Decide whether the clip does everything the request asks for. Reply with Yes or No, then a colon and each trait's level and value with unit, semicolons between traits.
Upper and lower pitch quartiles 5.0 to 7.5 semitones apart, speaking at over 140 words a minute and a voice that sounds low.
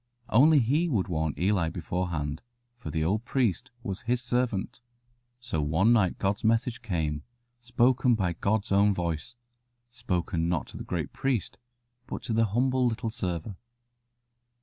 Yes: wide, 5.5 semitones; average, 150 wpm; low, 105 Hz